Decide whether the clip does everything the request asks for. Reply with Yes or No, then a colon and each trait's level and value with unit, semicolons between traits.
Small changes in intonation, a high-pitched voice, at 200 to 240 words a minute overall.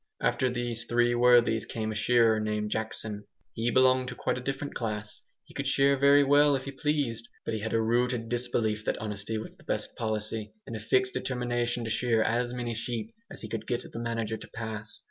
No: narrow, 2.1 semitones; low, 115 Hz; fast, 205 wpm